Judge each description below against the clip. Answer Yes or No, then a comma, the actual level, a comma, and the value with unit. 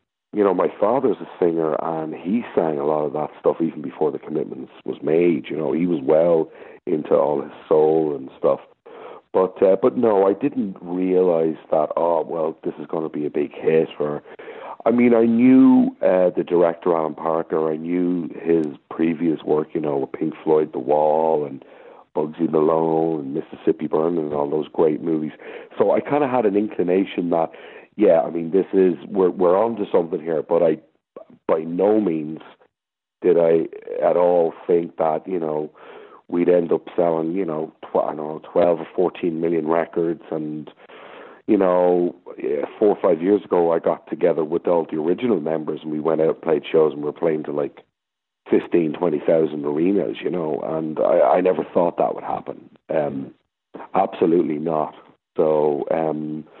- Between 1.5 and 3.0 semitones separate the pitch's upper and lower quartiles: Yes, narrow, 2.6 semitones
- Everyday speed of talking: Yes, average, 190 wpm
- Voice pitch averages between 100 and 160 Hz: No, very low, 80 Hz